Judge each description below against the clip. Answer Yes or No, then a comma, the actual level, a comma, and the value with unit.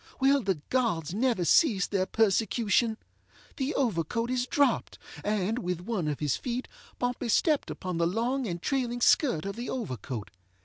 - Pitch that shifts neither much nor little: No, wide, 5.7 semitones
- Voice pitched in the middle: No, high, 225 Hz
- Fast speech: No, average, 160 wpm